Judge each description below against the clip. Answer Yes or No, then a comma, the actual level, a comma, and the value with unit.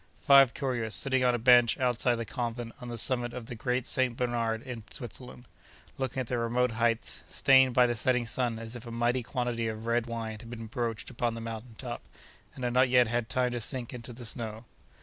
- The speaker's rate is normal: No, fast, 220 wpm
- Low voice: Yes, low, 120 Hz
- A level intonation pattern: Yes, narrow, 1.5 semitones